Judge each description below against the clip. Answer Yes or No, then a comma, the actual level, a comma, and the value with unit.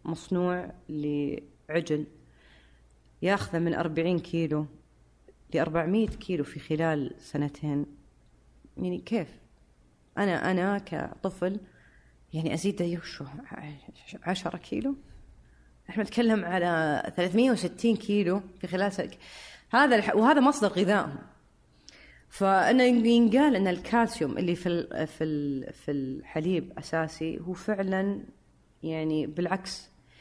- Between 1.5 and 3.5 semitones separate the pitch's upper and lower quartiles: No, average, 4.8 semitones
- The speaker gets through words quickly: No, average, 95 wpm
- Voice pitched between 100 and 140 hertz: No, medium, 170 Hz